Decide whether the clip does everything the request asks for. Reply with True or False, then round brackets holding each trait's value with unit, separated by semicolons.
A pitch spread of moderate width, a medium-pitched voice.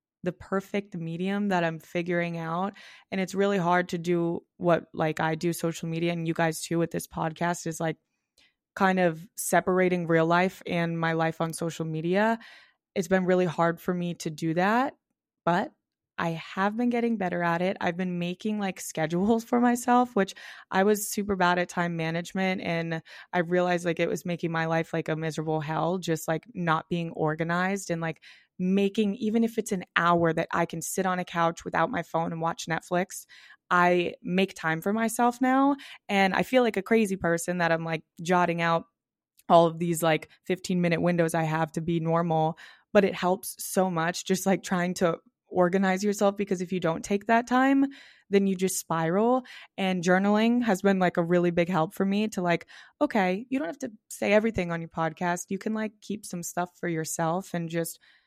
True (3.0 semitones; 180 Hz)